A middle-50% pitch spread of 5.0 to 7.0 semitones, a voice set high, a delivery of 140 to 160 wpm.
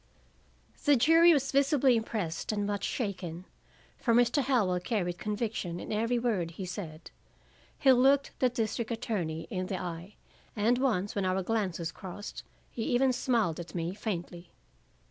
Yes: average, 5.3 semitones; high, 210 Hz; average, 150 wpm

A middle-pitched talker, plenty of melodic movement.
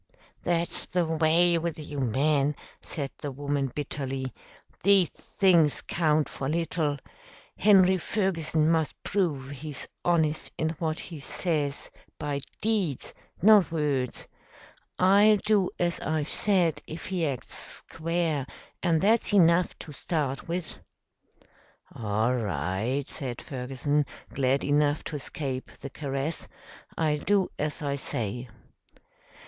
No: medium, 155 Hz; average, 3.8 semitones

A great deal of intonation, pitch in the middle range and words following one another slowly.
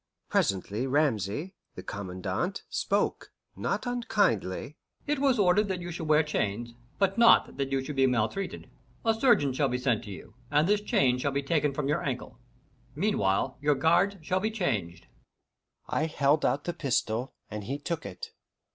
No: wide, 6.7 semitones; medium, 145 Hz; average, 165 wpm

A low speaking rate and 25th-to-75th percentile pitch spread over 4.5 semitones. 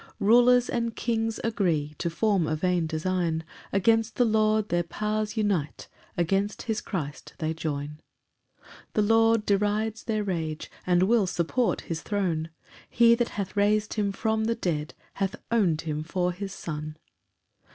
No: average, 155 wpm; average, 4.9 semitones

